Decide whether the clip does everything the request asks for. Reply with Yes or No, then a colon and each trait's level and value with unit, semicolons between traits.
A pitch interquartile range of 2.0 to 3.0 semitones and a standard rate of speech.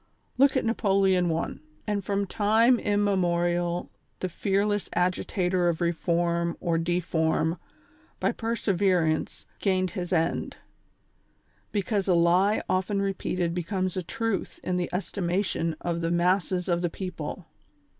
No: narrow, 2.5 semitones; slow, 125 wpm